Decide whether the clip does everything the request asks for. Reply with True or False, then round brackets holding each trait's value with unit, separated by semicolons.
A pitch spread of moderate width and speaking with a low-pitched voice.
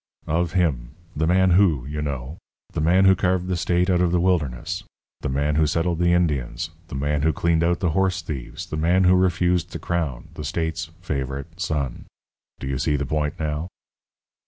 True (3.4 semitones; 80 Hz)